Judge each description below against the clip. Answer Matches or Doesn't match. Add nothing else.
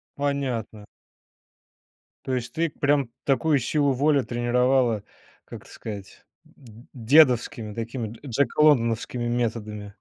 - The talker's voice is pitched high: Doesn't match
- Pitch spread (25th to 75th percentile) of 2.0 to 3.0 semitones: Doesn't match